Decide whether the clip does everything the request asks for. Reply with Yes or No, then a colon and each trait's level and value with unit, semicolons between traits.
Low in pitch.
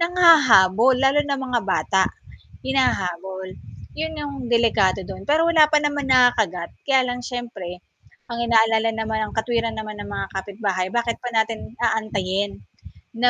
No: high, 230 Hz